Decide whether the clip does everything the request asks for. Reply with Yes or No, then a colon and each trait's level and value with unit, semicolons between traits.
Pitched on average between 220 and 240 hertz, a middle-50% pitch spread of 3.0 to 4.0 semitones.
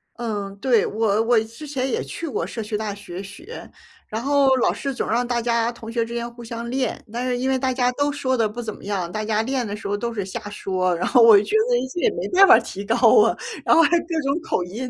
Yes: high, 235 Hz; average, 3.6 semitones